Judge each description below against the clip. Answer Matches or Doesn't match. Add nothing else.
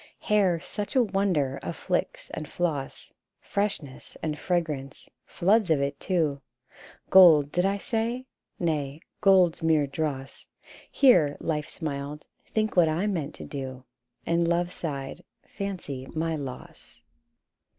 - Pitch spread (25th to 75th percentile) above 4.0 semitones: Matches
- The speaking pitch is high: Doesn't match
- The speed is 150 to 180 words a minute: Doesn't match